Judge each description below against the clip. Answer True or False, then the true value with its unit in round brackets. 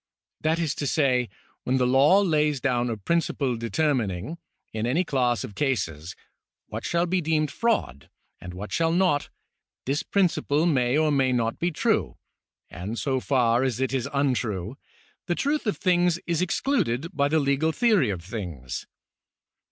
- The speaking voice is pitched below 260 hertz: True (140 Hz)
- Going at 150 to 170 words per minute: True (165 wpm)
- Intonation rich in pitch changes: True (5.7 semitones)